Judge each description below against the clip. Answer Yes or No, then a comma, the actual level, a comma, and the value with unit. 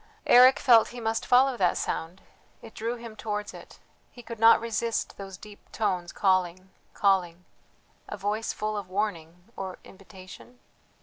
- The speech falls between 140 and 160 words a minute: Yes, average, 150 wpm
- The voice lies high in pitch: Yes, high, 210 Hz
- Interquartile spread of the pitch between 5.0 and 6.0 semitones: No, average, 3.6 semitones